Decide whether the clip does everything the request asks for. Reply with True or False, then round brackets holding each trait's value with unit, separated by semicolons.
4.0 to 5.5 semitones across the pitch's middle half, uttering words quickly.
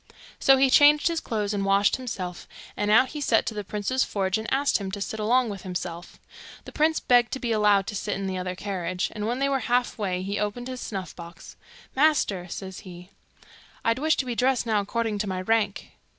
True (4.4 semitones; 220 wpm)